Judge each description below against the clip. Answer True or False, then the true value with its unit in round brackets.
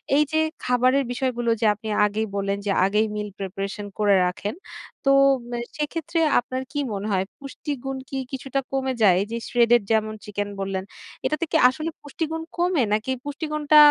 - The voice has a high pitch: True (245 Hz)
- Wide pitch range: True (5.8 semitones)